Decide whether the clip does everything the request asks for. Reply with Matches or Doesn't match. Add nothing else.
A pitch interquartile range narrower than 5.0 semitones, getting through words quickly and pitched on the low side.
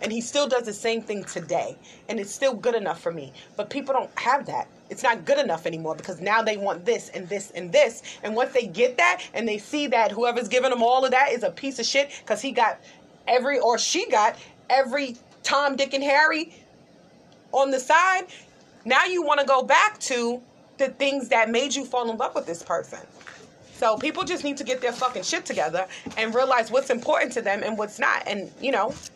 Doesn't match